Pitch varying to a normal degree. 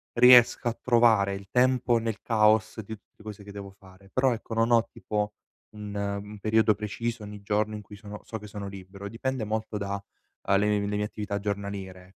No: narrow, 1.9 semitones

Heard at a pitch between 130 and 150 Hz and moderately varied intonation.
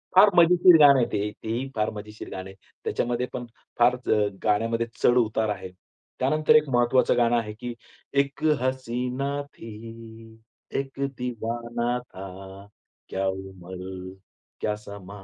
No: low, 115 Hz; average, 3.5 semitones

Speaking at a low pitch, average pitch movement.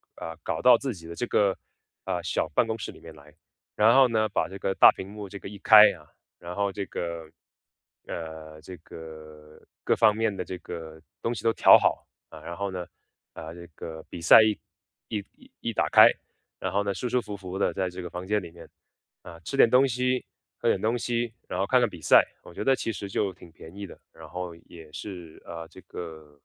Yes: very low, 95 Hz; average, 4.7 semitones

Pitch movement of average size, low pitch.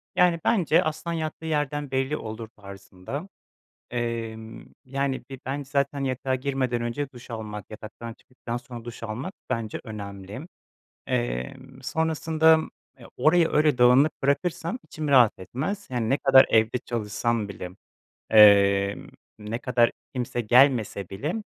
Yes: average, 4.7 semitones; low, 125 Hz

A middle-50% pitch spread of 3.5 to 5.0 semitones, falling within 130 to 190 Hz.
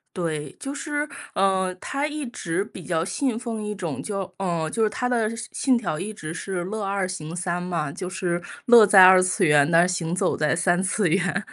Yes: average, 4.0 semitones; medium, 185 Hz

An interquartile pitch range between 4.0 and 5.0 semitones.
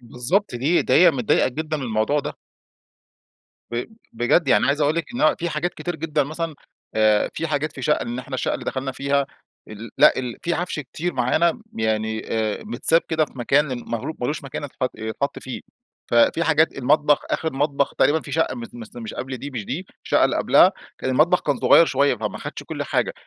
Yes: average, 4.6 semitones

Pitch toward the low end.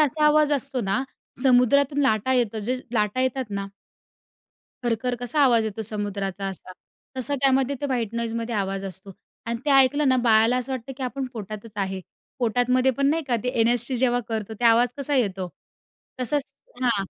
No: high, 245 Hz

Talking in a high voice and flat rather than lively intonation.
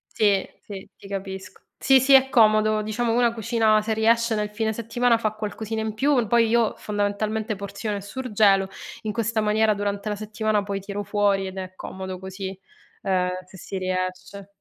Yes: high, 210 Hz; narrow, 2.1 semitones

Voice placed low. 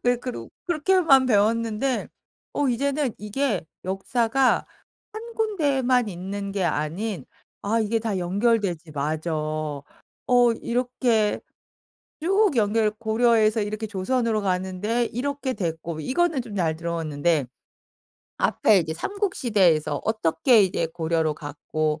No: high, 215 Hz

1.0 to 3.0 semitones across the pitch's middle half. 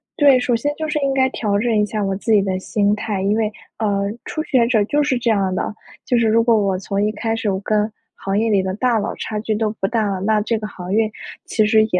Yes: narrow, 2.4 semitones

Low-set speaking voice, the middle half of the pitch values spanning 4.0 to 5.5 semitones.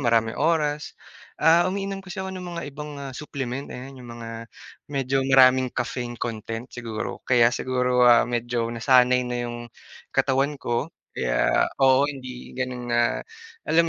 No: low, 130 Hz; average, 3.1 semitones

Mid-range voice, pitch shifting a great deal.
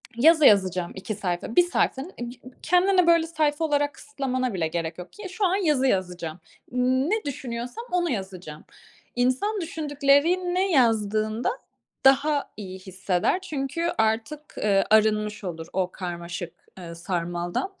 No: high, 245 Hz; wide, 8.7 semitones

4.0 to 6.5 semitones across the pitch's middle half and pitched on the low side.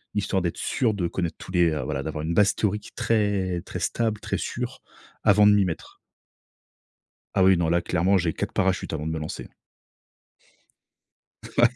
No: average, 3.6 semitones; very low, 95 Hz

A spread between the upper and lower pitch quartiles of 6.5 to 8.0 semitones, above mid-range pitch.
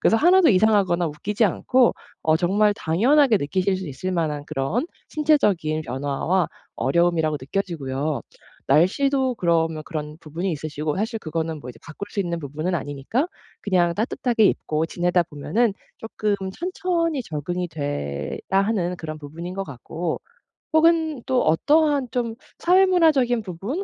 No: wide, 7.1 semitones; medium, 180 Hz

